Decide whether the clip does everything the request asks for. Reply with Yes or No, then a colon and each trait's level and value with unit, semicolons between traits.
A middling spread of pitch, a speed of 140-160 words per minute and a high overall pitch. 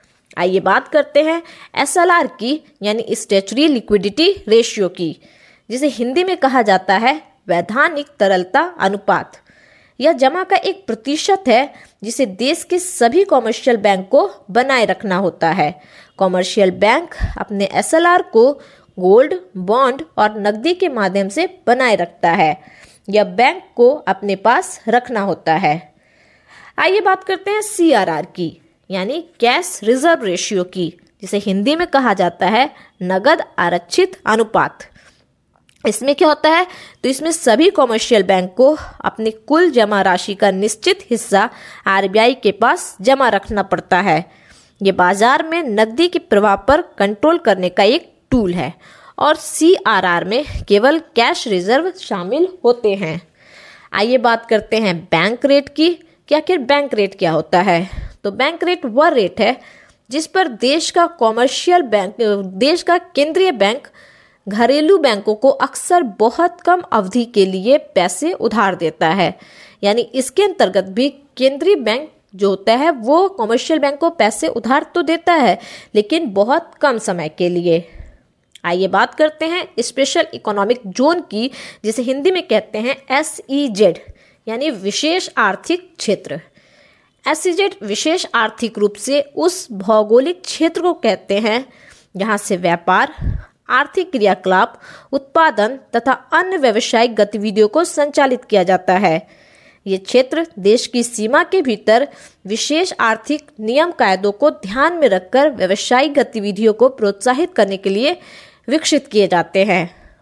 No: wide, 7.5 semitones; average, 145 wpm; high, 240 Hz